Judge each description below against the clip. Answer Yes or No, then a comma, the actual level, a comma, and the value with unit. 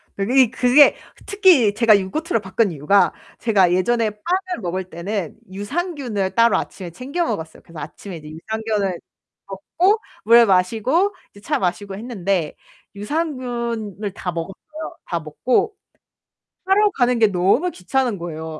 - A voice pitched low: No, high, 210 Hz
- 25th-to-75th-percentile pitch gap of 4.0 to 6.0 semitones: Yes, wide, 5.6 semitones